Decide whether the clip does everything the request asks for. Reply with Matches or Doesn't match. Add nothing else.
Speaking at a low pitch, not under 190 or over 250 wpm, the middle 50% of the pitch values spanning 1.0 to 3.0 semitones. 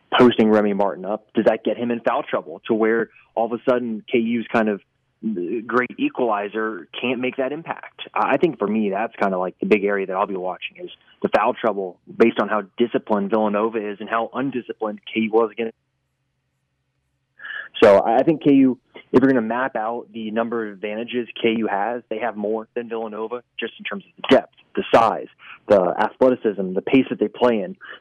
Matches